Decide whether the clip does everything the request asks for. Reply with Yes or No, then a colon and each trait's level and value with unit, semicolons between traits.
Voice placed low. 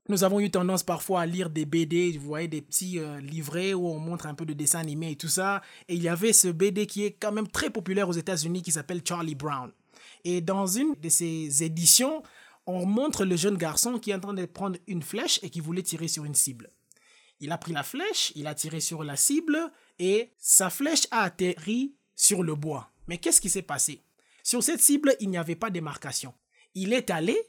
No: medium, 180 Hz